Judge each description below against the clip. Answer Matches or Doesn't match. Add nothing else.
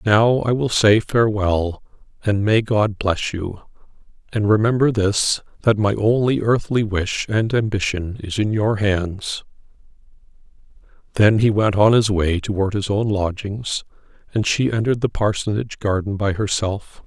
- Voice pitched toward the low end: Matches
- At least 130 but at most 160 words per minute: Matches